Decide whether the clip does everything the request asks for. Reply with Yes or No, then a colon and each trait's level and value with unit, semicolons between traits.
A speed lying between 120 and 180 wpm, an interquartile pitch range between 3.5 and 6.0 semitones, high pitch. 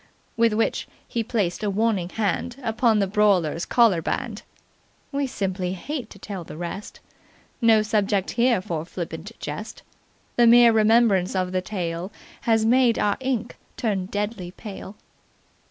Yes: average, 140 wpm; average, 3.8 semitones; high, 210 Hz